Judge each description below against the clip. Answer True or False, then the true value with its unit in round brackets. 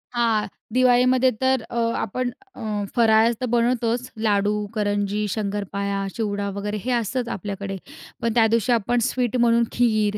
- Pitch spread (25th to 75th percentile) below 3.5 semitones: True (3.0 semitones)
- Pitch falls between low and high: False (225 Hz)